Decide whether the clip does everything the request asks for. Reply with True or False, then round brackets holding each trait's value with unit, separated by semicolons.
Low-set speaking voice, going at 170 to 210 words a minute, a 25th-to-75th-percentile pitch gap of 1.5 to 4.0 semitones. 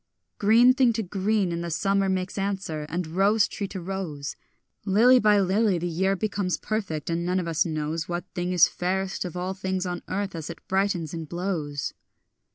False (185 Hz; 190 wpm; 2.9 semitones)